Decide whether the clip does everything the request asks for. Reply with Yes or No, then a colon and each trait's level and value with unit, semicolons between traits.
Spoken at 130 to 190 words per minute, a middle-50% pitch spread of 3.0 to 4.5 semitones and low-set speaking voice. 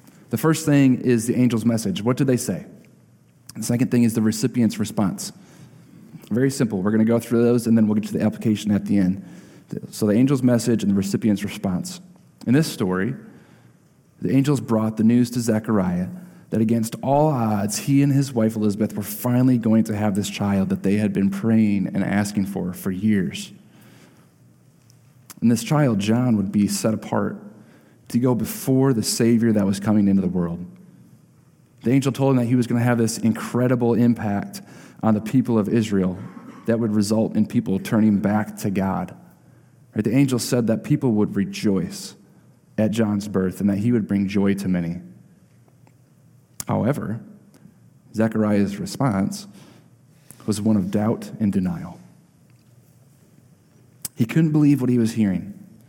Yes: average, 170 wpm; average, 3.8 semitones; low, 115 Hz